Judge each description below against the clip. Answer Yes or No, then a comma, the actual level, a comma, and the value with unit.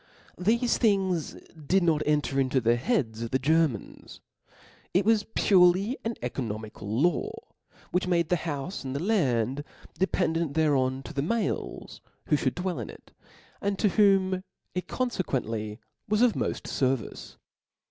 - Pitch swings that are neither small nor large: No, wide, 6.6 semitones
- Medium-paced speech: Yes, average, 145 wpm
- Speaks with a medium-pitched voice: Yes, medium, 165 Hz